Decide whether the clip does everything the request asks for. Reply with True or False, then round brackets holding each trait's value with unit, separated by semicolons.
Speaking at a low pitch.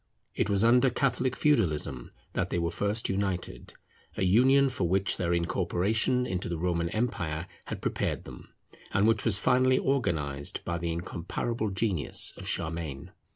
True (95 Hz)